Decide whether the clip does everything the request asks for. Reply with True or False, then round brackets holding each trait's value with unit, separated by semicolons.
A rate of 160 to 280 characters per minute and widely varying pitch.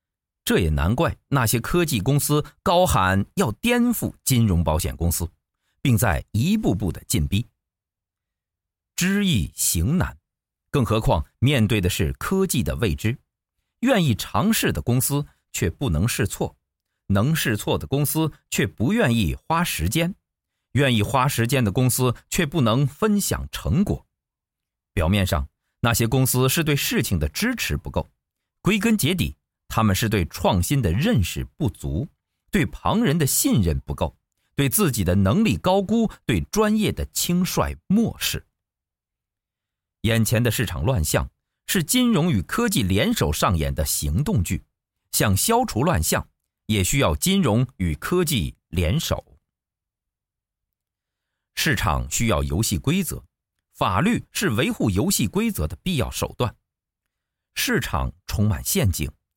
True (205 characters per minute; 8.9 semitones)